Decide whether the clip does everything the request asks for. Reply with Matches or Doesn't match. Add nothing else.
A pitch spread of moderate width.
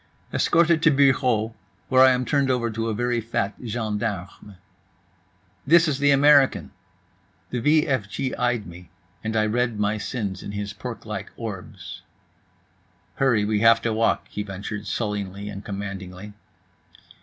Matches